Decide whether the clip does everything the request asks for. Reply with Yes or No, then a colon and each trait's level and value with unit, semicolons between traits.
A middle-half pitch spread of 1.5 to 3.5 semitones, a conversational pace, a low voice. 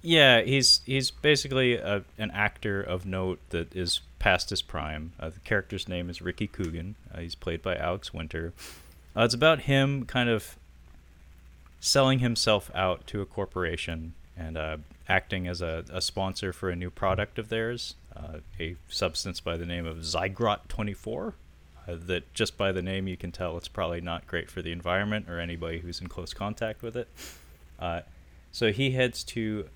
No: average, 4.7 semitones; average, 180 wpm; very low, 90 Hz